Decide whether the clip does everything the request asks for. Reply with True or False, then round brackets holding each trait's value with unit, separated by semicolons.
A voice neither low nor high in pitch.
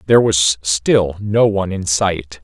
False (95 Hz)